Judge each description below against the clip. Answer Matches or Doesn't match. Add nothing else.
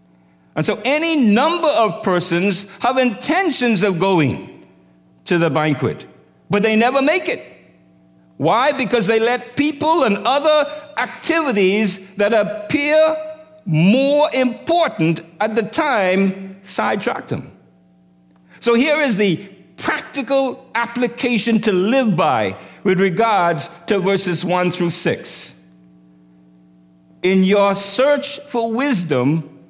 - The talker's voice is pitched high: Matches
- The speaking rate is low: Matches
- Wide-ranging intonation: Matches